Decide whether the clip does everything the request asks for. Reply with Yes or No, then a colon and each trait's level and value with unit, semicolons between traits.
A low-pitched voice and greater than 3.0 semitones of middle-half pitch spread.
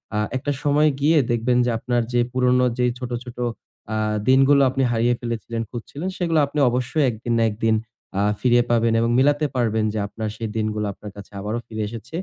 No: low, 120 Hz; average, 2.7 semitones